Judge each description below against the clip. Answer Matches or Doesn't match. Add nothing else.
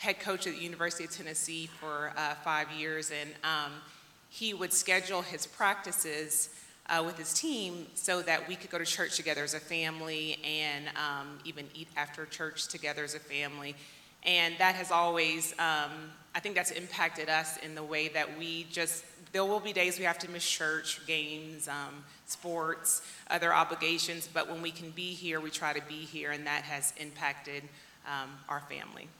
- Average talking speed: Matches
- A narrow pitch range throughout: Matches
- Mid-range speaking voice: Matches